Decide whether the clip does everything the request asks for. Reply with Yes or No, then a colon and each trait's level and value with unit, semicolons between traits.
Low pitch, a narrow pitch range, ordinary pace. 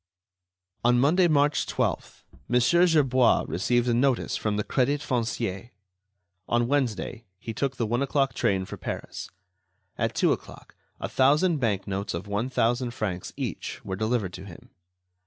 No: low, 120 Hz; average, 4.6 semitones; average, 155 wpm